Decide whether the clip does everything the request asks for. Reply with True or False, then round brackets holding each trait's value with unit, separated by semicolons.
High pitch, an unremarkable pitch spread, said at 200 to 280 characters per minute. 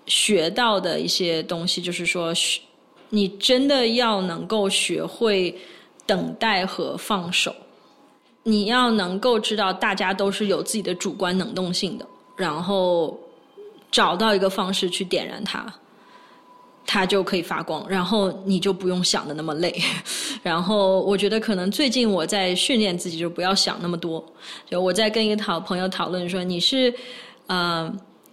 True (195 Hz; 3.2 semitones; 230 characters per minute)